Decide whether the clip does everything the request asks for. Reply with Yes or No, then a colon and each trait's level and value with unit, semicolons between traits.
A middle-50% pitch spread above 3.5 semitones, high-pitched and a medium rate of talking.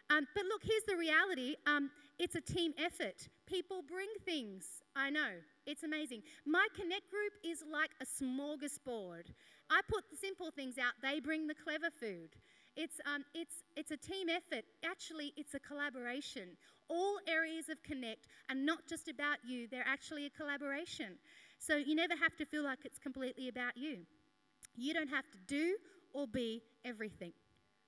Yes: average, 3.9 semitones; very high, 300 Hz; average, 170 wpm